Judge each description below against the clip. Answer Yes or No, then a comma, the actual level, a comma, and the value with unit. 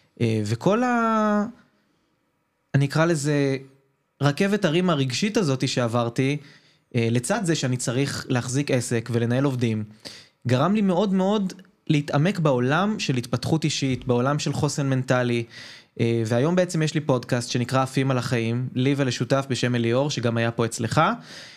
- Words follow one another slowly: No, average, 135 wpm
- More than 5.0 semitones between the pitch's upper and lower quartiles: No, average, 4.4 semitones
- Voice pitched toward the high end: No, low, 135 Hz